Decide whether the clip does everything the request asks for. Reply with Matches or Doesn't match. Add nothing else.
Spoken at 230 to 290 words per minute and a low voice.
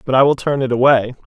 Matches